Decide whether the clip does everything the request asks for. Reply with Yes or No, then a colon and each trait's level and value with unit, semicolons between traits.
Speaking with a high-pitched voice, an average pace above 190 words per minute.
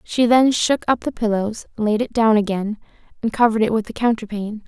Yes: high, 220 Hz; fast, 205 wpm